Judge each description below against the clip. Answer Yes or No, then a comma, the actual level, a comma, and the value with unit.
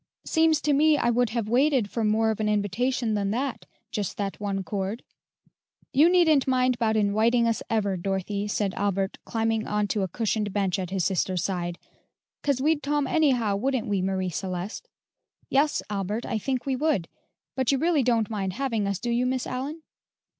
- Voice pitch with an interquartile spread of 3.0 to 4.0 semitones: No, average, 4.7 semitones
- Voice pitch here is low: No, high, 225 Hz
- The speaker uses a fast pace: No, average, 185 wpm